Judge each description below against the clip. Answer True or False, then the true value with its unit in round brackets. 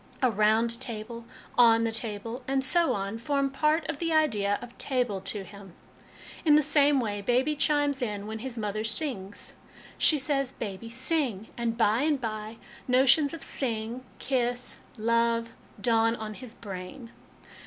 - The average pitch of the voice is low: False (235 Hz)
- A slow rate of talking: False (175 wpm)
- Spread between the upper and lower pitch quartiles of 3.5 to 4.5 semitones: True (4.0 semitones)